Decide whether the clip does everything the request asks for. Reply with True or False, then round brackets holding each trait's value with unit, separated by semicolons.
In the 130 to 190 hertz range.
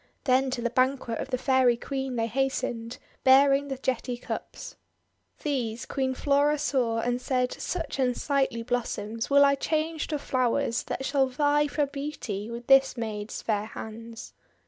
False (260 Hz)